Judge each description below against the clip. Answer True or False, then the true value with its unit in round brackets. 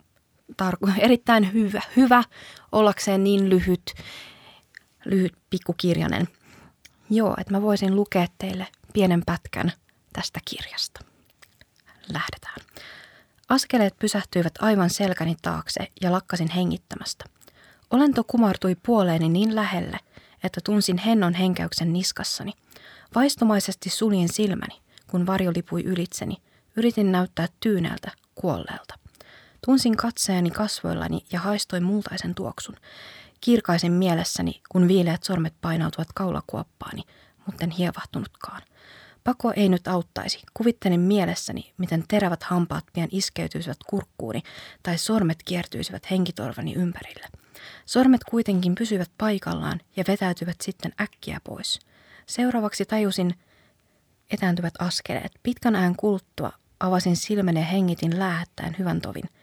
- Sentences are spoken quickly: False (105 wpm)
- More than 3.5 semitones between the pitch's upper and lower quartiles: False (3.1 semitones)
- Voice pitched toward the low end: False (190 Hz)